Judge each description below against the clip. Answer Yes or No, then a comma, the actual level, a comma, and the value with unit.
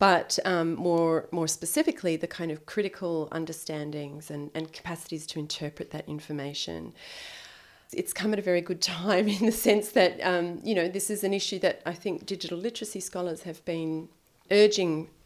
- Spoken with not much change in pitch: No, average, 3.5 semitones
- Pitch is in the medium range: Yes, medium, 170 Hz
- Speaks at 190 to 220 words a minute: No, average, 175 wpm